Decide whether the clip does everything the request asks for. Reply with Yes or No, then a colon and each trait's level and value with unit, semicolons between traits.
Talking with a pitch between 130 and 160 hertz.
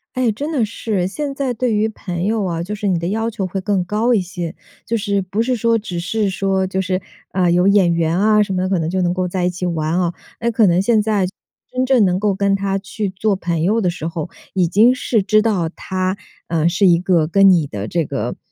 No: high, 195 Hz